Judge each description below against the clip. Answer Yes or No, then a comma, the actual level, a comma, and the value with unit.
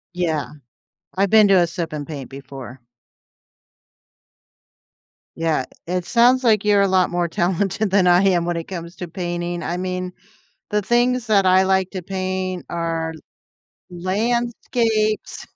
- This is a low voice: No, medium, 185 Hz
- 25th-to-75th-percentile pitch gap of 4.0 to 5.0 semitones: No, average, 2.8 semitones